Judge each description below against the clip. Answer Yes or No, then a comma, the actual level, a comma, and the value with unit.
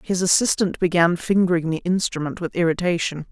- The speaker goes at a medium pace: Yes, average, 145 wpm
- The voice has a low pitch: No, medium, 175 Hz